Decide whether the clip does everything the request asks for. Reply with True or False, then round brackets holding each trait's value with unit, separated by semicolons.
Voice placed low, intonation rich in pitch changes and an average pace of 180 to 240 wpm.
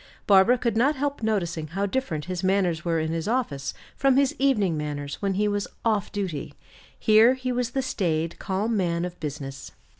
False (195 Hz; 6.1 semitones; 185 wpm)